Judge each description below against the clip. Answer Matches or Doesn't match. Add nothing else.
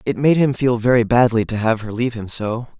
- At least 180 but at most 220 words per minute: Doesn't match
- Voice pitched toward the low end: Matches